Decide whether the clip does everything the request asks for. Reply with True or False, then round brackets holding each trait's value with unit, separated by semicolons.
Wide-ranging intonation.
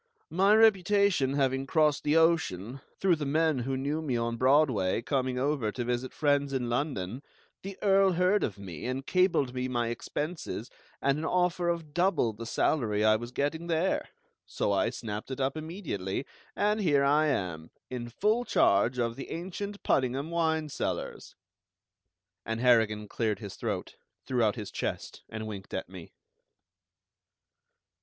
True (5.9 semitones)